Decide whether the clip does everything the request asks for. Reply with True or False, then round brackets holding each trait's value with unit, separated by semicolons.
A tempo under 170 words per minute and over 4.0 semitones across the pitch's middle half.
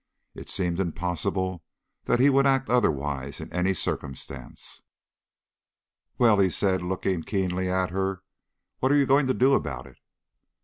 True (145 wpm; 5.6 semitones)